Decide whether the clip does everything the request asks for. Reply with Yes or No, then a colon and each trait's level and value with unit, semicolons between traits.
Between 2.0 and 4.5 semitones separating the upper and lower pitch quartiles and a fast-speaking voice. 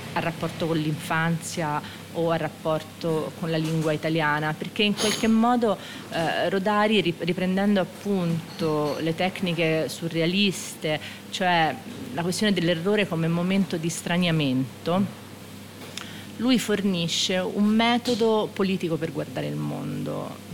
No: average, 4.0 semitones; slow, 115 wpm